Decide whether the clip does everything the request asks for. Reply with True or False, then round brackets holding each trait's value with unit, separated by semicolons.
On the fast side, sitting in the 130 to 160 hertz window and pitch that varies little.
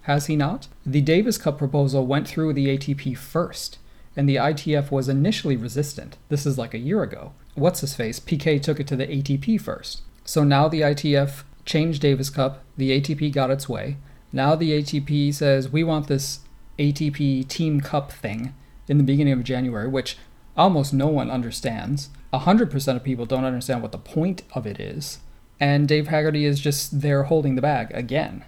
False (185 wpm; 140 Hz; 2.1 semitones)